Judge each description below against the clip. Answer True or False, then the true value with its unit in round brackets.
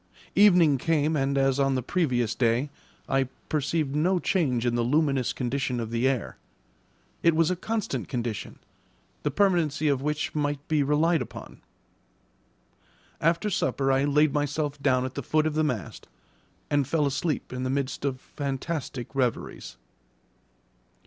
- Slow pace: False (150 wpm)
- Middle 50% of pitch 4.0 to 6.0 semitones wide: False (3.2 semitones)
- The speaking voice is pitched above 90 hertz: True (140 Hz)